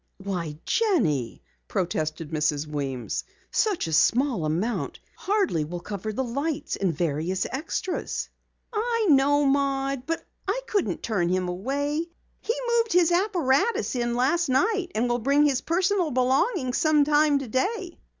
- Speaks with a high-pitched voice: Yes, very high, 270 Hz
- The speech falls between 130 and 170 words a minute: Yes, slow, 135 wpm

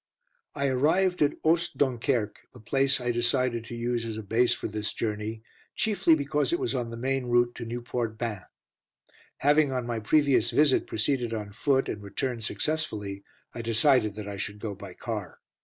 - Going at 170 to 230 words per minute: Yes, average, 180 wpm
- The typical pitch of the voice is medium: No, low, 120 Hz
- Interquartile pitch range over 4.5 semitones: No, average, 3.9 semitones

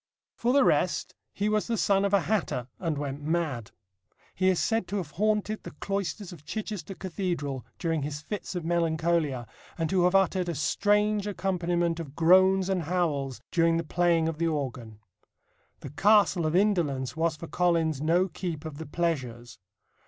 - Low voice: No, medium, 170 Hz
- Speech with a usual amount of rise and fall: Yes, average, 4.0 semitones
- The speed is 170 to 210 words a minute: Yes, average, 175 wpm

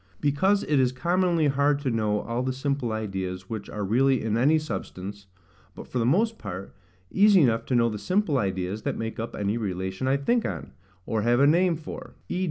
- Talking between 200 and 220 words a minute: Yes, fast, 205 wpm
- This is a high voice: No, low, 125 Hz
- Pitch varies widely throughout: Yes, wide, 6.1 semitones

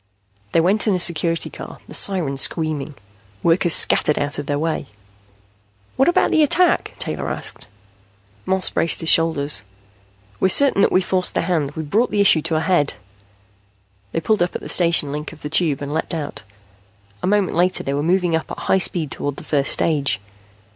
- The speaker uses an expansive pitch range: No, average, 3.8 semitones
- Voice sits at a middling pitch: Yes, medium, 165 Hz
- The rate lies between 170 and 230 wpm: Yes, average, 190 wpm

